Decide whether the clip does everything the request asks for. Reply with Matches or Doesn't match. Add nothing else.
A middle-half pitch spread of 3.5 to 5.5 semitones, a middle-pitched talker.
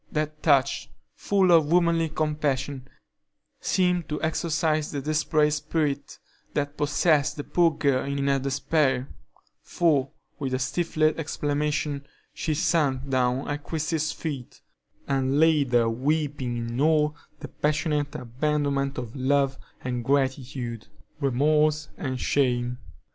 Doesn't match